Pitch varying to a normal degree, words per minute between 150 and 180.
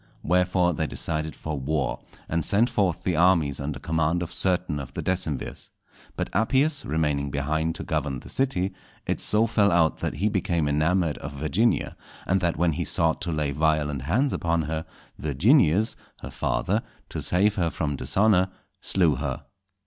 Yes: average, 3.8 semitones; average, 170 wpm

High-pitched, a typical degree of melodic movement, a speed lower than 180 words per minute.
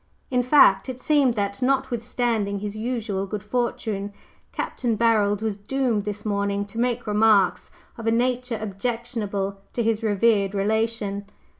Yes: high, 220 Hz; average, 3.0 semitones; average, 140 wpm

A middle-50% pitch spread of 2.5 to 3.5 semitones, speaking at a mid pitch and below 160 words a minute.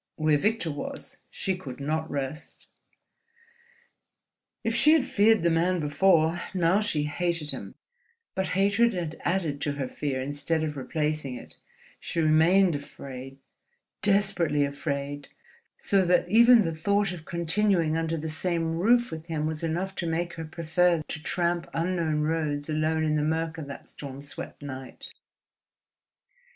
Yes: average, 3.2 semitones; medium, 160 Hz; average, 150 wpm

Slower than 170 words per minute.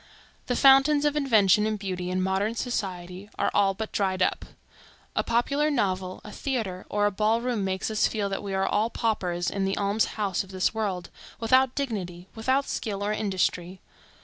No: average, 185 wpm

